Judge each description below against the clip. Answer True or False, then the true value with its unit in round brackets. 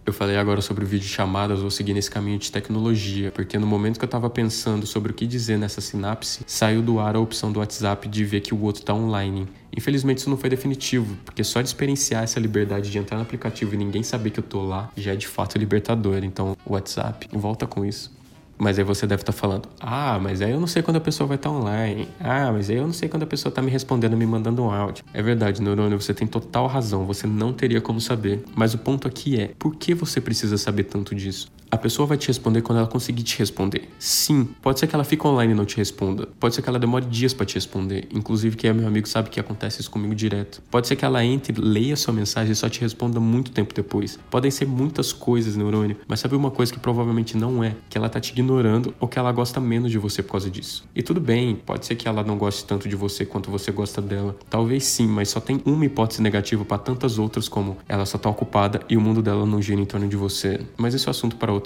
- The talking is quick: True (260 wpm)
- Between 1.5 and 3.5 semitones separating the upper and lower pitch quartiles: True (3.2 semitones)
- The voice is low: True (110 Hz)